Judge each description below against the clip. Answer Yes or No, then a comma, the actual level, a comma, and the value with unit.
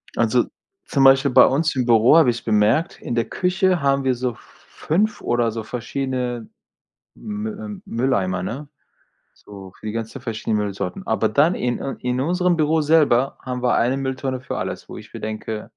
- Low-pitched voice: Yes, low, 130 Hz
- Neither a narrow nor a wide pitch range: Yes, average, 4.5 semitones